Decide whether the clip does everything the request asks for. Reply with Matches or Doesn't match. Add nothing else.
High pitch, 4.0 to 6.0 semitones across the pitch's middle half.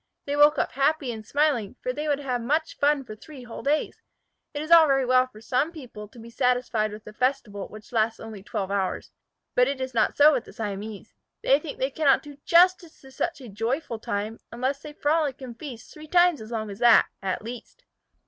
Matches